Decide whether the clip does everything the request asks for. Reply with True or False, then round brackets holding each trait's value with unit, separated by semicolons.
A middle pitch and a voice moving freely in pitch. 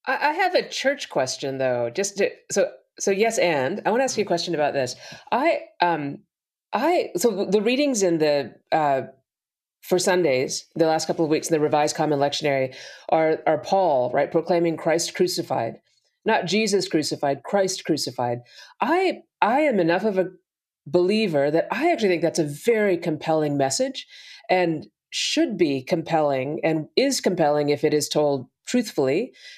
True (170 Hz; 6.2 semitones)